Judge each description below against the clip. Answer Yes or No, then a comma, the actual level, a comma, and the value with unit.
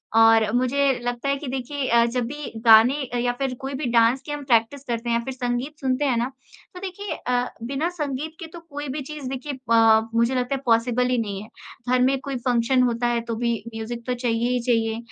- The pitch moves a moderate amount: Yes, average, 3.0 semitones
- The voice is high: Yes, very high, 250 Hz